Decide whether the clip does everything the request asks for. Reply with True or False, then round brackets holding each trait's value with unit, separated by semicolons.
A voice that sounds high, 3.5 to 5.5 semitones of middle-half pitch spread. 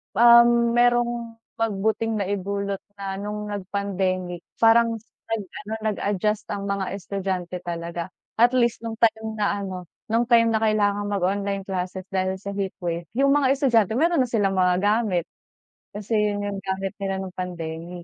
False (200 Hz; 3.0 semitones)